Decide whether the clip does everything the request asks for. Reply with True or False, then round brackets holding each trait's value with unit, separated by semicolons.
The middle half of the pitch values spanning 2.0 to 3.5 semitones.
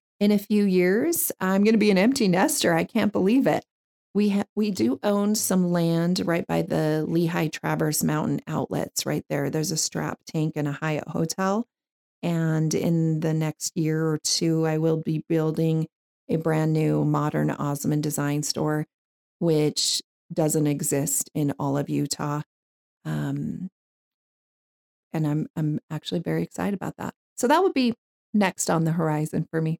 False (3.9 semitones)